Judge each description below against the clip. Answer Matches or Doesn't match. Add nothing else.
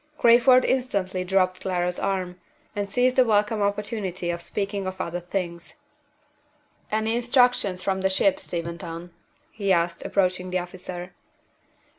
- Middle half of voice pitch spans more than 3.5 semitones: Doesn't match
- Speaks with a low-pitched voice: Doesn't match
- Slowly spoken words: Matches